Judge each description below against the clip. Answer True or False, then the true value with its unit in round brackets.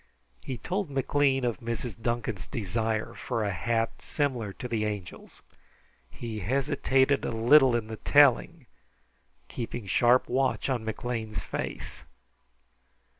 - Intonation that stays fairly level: False (3.2 semitones)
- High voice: False (120 Hz)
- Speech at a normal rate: False (125 wpm)